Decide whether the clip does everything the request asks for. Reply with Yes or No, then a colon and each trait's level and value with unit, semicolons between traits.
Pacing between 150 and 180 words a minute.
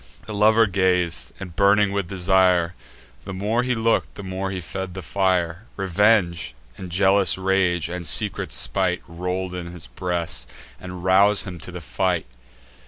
Yes: average, 160 wpm